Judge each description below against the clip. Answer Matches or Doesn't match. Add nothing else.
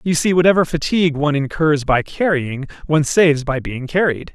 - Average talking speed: Matches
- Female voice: Doesn't match